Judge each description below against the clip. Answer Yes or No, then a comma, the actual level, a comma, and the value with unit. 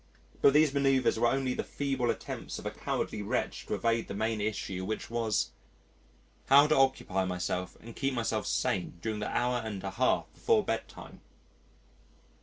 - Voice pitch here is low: Yes, low, 115 Hz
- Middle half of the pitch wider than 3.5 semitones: Yes, average, 4.6 semitones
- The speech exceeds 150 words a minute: Yes, average, 170 wpm